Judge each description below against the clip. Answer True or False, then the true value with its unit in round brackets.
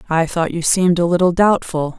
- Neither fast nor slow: False (210 wpm)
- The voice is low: False (170 Hz)